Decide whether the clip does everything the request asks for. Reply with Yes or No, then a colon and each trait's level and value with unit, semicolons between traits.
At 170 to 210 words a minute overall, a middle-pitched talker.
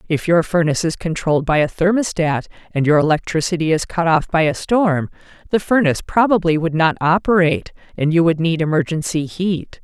Yes: average, 175 wpm; medium, 165 Hz